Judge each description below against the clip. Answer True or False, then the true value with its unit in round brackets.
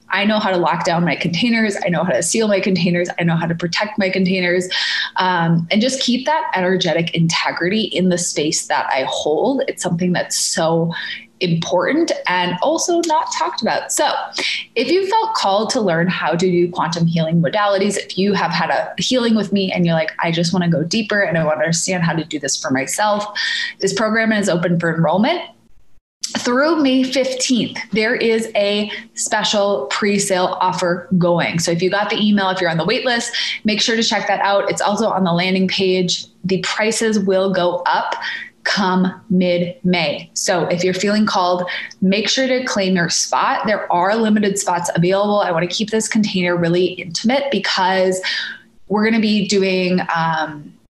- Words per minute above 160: True (195 wpm)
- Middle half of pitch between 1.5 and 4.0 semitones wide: True (3.7 semitones)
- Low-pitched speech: False (190 Hz)